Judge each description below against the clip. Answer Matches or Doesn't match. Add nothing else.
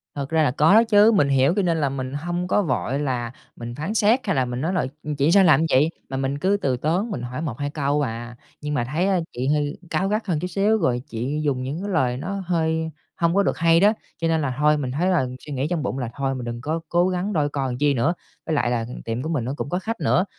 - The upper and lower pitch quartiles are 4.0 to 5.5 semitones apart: Matches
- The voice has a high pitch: Doesn't match